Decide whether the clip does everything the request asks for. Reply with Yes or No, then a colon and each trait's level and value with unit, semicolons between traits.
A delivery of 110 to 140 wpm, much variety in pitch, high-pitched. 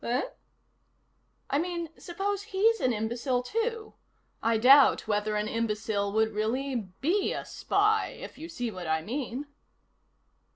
Yes: slow, 135 wpm; wide, 8.1 semitones; very high, 250 Hz